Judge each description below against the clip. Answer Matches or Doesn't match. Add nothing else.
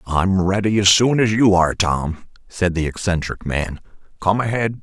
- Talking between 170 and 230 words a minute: Matches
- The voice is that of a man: Matches